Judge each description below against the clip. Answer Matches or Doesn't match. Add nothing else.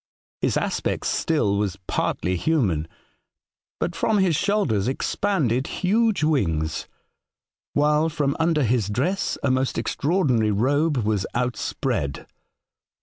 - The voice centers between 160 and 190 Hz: Doesn't match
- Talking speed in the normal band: Doesn't match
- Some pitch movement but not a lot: Doesn't match